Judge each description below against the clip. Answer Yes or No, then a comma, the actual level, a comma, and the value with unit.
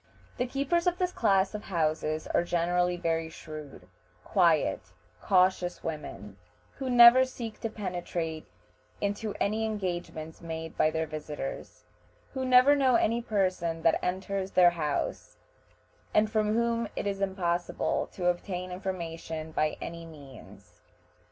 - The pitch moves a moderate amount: Yes, average, 4.9 semitones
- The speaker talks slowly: Yes, slow, 130 wpm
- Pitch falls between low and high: Yes, medium, 180 Hz